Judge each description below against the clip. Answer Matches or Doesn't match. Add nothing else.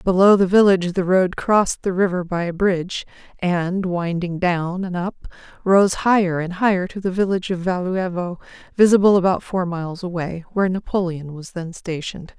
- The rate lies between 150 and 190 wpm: Matches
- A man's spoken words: Doesn't match